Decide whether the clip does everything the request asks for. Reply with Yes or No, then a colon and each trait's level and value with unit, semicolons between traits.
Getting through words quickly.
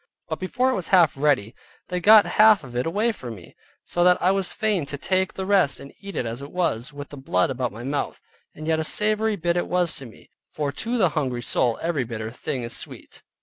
Yes: fast, 240 wpm